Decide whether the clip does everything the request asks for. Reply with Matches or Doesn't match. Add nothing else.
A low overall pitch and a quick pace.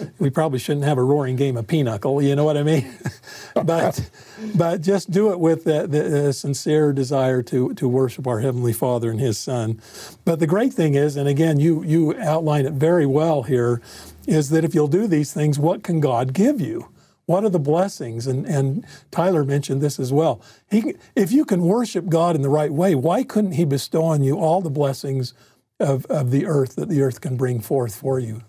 Doesn't match